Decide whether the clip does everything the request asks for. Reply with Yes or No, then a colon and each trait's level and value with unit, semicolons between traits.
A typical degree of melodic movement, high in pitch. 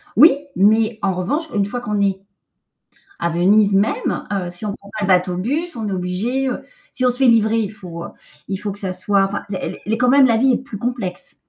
Yes: average, 4.0 semitones; high, 205 Hz